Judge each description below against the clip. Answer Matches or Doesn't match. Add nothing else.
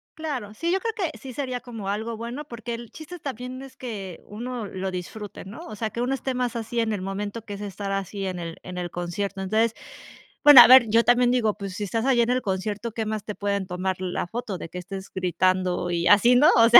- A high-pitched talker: Matches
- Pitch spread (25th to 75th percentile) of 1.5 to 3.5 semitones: Doesn't match